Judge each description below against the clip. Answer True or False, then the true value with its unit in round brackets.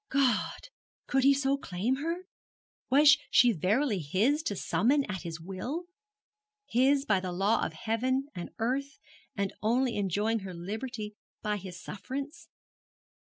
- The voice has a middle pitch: False (225 Hz)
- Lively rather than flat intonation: True (5.8 semitones)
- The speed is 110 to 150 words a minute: True (140 wpm)